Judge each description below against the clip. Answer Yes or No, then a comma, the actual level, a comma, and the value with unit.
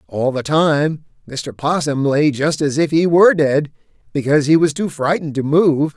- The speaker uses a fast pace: No, average, 190 wpm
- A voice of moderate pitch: Yes, medium, 150 Hz